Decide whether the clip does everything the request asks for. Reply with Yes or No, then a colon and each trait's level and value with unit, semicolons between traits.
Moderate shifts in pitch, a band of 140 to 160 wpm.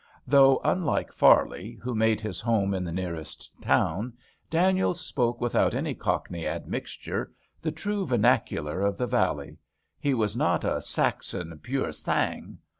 No: wide, 5.8 semitones; average, 150 wpm